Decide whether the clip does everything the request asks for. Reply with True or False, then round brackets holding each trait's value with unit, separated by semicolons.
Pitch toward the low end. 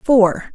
False (220 Hz)